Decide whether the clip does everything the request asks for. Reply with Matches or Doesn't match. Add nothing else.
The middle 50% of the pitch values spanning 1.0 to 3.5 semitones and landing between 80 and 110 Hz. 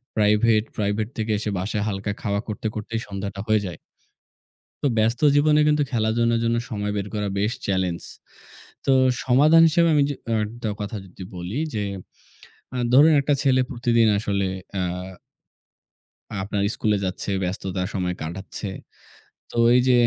Matches